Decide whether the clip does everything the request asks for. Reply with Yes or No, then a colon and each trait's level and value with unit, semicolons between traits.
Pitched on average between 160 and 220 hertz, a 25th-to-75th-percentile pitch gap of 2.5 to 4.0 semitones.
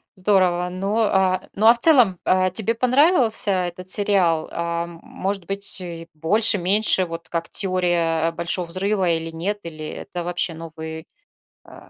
Yes: medium, 185 Hz; average, 3.1 semitones